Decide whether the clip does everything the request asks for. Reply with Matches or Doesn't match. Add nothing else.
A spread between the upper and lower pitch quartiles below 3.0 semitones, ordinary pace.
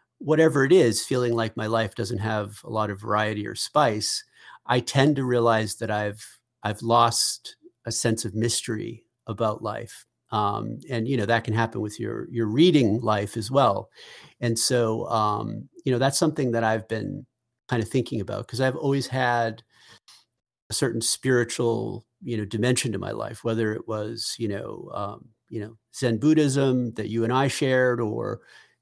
Matches